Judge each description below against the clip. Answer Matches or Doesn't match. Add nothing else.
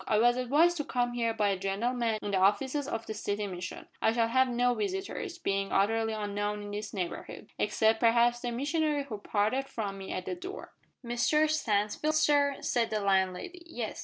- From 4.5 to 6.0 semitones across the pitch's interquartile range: Matches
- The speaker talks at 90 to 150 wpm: Doesn't match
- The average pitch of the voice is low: Doesn't match